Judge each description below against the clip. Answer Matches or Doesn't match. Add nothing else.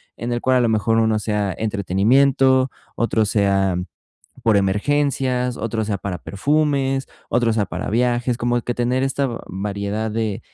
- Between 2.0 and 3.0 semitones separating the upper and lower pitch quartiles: Doesn't match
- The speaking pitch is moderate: Doesn't match